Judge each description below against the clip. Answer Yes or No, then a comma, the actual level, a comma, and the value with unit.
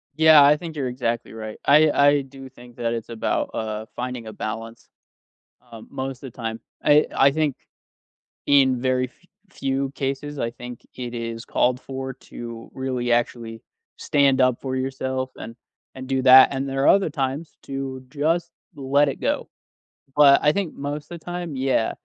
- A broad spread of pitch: No, average, 2.8 semitones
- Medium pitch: No, low, 130 Hz